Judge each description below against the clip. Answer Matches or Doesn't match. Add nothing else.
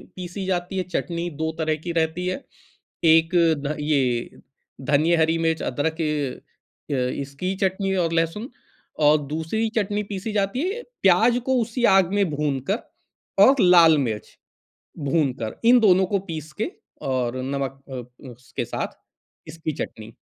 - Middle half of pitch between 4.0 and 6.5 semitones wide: Matches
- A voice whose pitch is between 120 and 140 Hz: Doesn't match